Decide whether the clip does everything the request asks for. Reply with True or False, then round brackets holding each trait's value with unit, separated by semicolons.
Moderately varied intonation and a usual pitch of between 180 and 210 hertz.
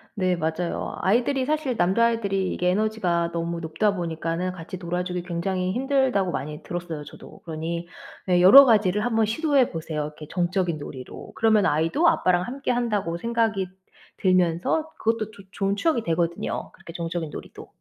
True (4.8 semitones; 185 Hz)